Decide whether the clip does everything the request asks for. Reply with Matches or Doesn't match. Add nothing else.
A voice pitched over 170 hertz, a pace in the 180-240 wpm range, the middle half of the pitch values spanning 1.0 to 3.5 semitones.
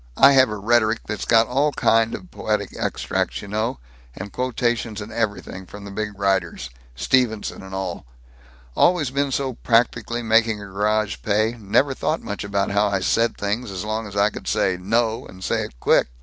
Doesn't match